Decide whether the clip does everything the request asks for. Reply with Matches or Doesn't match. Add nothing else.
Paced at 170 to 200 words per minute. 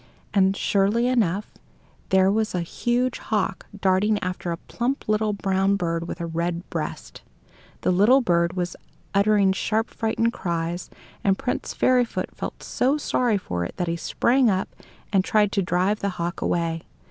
Doesn't match